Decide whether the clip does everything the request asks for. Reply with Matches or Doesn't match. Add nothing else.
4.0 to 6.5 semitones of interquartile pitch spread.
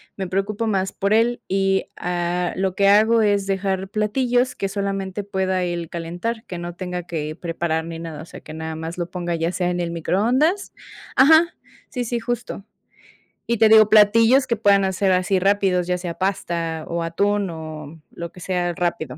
Doesn't match